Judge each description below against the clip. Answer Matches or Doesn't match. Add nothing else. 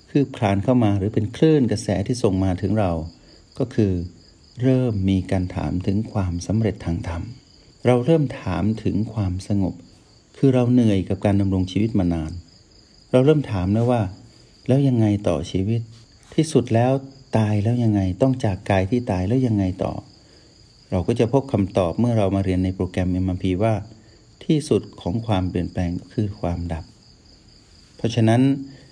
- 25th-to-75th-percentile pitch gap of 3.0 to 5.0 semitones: Matches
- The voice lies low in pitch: Matches